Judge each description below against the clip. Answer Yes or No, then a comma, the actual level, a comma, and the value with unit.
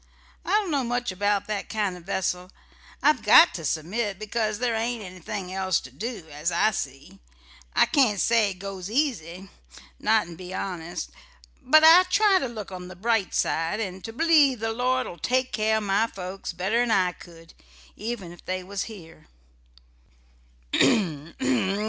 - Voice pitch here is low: No, high, 205 Hz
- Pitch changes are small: No, average, 4.6 semitones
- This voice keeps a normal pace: Yes, average, 160 wpm